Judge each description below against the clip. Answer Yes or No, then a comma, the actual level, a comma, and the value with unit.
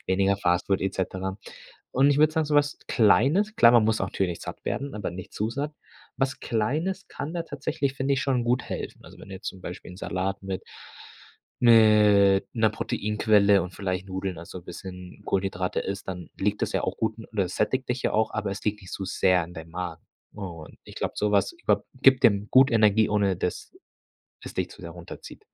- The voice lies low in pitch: Yes, low, 105 Hz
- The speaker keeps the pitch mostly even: No, average, 4.8 semitones